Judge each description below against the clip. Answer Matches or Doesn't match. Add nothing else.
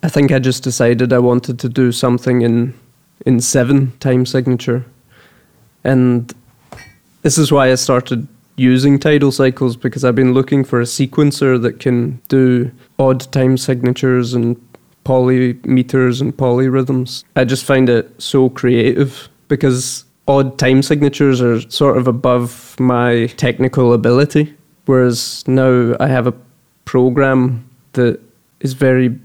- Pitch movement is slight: Matches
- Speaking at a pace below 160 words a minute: Matches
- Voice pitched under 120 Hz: Doesn't match